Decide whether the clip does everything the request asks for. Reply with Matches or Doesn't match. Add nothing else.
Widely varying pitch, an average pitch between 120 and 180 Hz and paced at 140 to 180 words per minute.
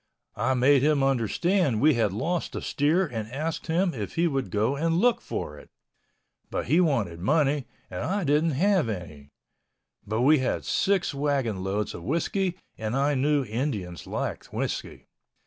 Matches